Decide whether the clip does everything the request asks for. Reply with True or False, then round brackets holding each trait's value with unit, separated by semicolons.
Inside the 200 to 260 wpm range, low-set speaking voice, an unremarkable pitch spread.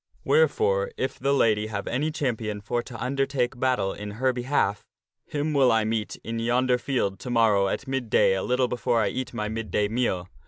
True (205 wpm; 120 Hz; 3.7 semitones)